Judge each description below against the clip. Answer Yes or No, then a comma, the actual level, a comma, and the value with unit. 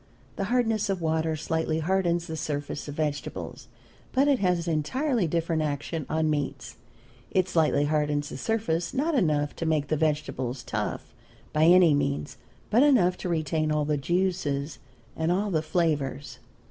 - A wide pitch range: No, average, 3.6 semitones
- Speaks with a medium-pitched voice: Yes, medium, 160 Hz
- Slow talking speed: No, average, 160 wpm